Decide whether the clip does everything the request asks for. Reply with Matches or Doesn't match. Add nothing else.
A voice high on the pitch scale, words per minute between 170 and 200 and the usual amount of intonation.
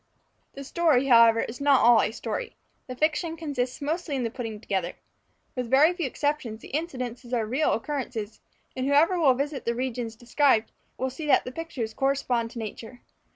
Matches